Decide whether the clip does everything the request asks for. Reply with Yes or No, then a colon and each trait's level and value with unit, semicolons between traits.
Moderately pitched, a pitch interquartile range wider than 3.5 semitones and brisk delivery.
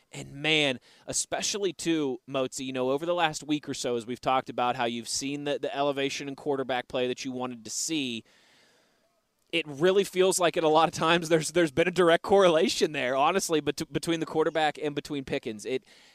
Yes: medium, 150 Hz; average, 4.0 semitones; fast, 210 wpm